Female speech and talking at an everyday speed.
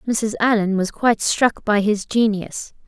Yes: female; average, 165 wpm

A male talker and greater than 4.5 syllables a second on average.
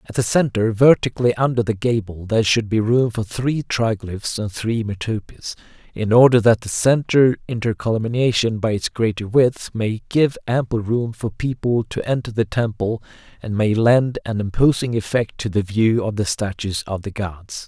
Yes: male; 4.8 syllables/s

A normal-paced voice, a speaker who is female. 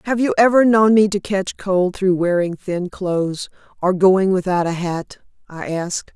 Yes: average, 185 wpm; female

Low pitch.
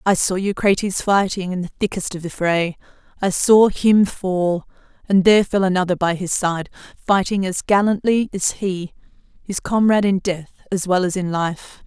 No: high, 190 Hz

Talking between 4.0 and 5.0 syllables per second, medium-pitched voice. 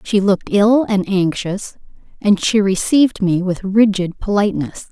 No: 4.6 syllables/s; high, 200 Hz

